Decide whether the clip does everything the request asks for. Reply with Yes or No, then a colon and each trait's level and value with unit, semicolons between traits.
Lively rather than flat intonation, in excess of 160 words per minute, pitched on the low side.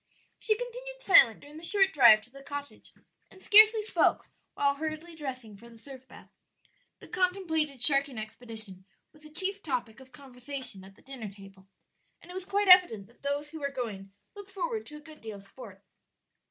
No: wide, 7.9 semitones; average, 190 wpm; very high, 280 Hz